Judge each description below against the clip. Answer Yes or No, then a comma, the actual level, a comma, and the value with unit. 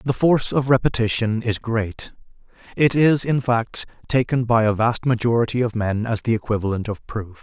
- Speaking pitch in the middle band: No, low, 115 Hz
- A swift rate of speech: No, average, 180 wpm